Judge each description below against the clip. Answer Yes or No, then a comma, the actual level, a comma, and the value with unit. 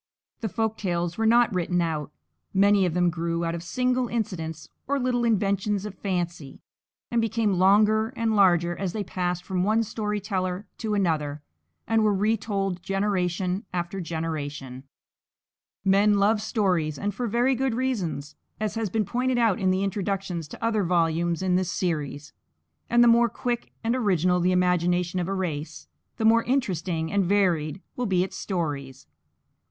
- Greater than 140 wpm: Yes, average, 165 wpm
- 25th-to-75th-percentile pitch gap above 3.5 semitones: Yes, average, 4.0 semitones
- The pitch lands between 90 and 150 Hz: No, high, 190 Hz